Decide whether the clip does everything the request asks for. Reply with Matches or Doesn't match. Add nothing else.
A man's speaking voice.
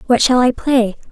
Doesn't match